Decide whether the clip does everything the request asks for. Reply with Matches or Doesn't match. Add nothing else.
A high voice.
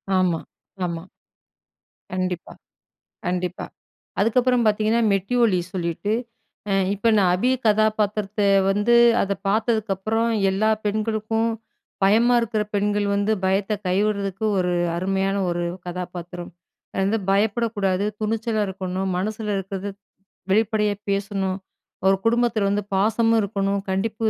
Matches